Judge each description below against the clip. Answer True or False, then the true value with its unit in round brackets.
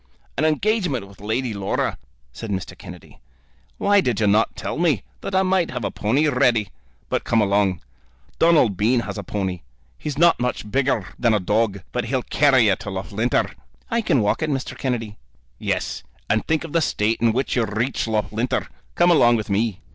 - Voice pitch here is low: True (115 Hz)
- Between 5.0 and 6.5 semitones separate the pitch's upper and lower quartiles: True (5.3 semitones)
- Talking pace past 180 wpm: True (190 wpm)